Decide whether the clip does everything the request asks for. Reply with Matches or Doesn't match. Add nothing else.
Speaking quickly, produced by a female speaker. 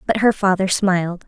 Doesn't match